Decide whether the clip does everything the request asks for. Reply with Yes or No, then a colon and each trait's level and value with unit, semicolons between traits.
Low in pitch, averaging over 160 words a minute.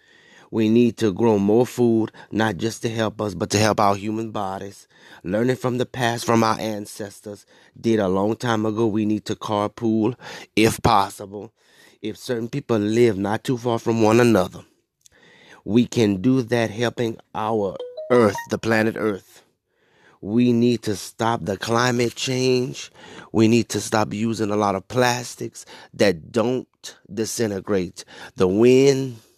No: low, 110 Hz; average, 155 wpm